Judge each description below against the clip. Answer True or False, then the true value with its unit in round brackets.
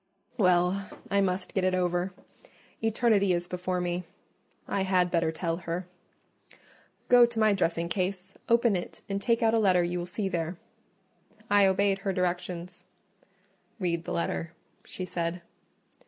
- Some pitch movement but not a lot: False (2.1 semitones)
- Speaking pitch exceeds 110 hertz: True (185 Hz)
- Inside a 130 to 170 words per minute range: True (145 wpm)